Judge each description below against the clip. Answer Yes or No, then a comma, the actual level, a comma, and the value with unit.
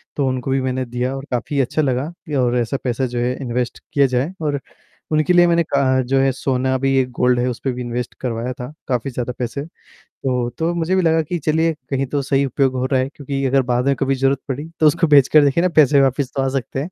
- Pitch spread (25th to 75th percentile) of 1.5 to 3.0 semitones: Yes, narrow, 2.4 semitones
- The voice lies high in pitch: No, low, 135 Hz